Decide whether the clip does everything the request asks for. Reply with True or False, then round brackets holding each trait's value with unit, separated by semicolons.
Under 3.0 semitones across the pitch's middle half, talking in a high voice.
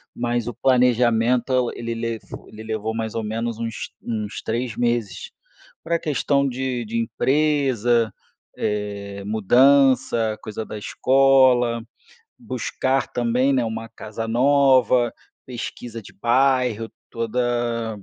False (2.4 semitones; 120 Hz)